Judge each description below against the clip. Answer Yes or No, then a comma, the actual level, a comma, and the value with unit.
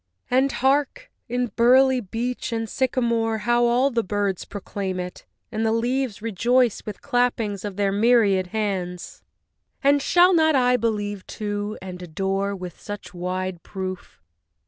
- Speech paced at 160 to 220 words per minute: No, average, 145 wpm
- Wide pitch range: No, average, 4.2 semitones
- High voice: Yes, high, 220 Hz